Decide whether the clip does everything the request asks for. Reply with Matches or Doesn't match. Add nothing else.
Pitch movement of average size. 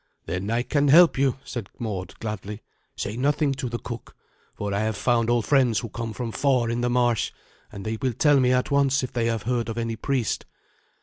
Matches